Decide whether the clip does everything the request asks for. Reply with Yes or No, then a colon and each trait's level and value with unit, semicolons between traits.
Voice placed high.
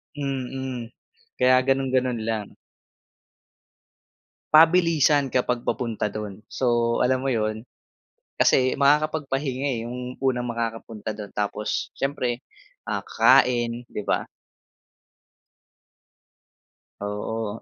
No: low, 125 Hz